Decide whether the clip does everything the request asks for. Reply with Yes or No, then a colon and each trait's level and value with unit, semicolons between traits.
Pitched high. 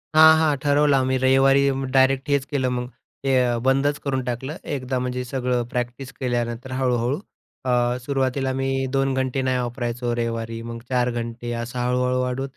No: low, 130 Hz